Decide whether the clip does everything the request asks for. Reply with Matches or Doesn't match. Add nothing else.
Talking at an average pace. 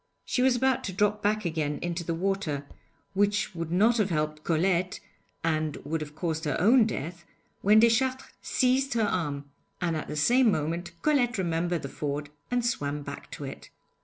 Matches